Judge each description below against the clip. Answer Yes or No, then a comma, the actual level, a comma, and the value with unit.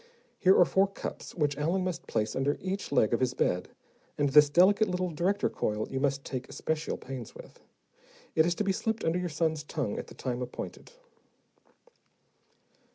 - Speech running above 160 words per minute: Yes, average, 180 wpm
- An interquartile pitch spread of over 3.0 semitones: Yes, wide, 5.5 semitones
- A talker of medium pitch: Yes, medium, 155 Hz